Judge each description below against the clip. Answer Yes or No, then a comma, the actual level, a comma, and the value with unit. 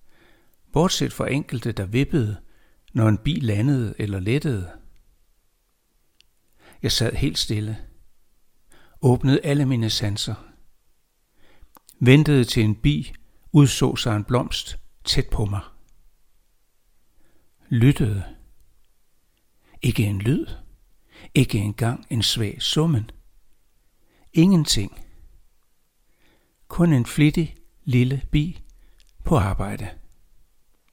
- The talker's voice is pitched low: Yes, low, 115 Hz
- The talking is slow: Yes, slow, 90 wpm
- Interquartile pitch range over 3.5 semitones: Yes, average, 5.2 semitones